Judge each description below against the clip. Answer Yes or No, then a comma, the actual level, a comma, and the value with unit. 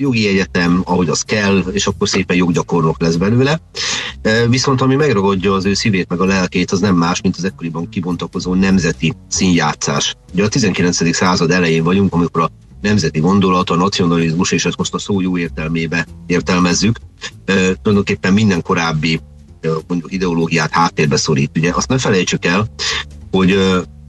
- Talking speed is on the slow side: No, average, 150 wpm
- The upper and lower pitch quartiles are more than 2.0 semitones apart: Yes, narrow, 2.6 semitones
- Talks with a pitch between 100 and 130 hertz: No, very low, 90 Hz